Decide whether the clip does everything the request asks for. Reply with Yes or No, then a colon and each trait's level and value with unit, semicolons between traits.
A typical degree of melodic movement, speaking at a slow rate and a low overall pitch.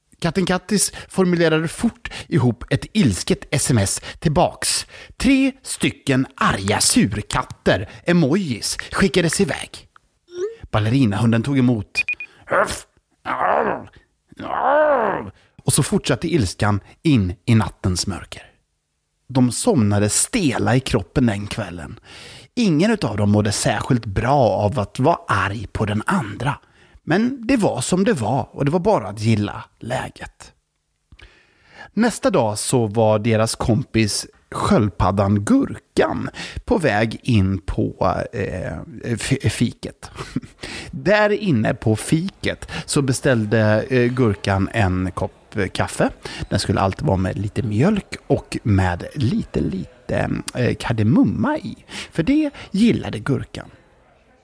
No: wide, 8.4 semitones; slow, 110 wpm; low, 115 Hz